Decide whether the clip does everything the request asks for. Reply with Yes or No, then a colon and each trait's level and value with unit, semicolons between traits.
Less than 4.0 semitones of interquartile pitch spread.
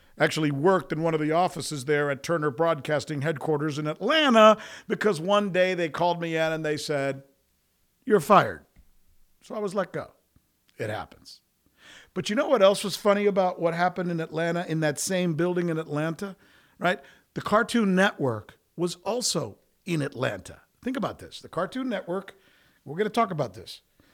No: average, 4.8 semitones